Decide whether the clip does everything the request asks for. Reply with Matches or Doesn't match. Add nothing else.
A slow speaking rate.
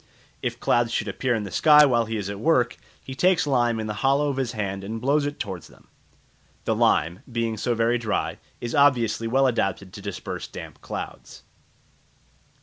Doesn't match